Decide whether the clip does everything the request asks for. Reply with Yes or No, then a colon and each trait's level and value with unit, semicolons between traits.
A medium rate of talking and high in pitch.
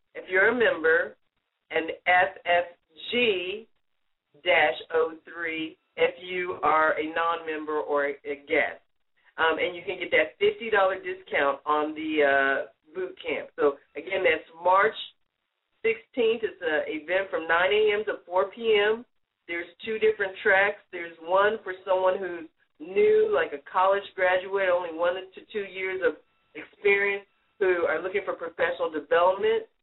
Yes: average, 145 wpm; high, 195 Hz